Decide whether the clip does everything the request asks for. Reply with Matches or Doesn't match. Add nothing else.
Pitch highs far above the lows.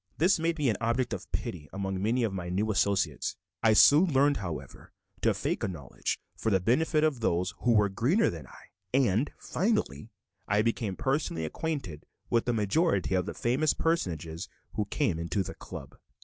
Matches